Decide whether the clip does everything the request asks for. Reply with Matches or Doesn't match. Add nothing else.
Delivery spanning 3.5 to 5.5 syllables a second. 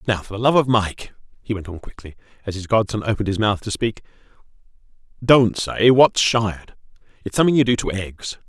Doesn't match